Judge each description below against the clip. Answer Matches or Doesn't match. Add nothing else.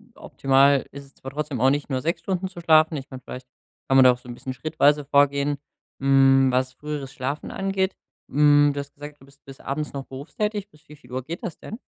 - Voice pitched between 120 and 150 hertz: Matches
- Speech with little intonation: Matches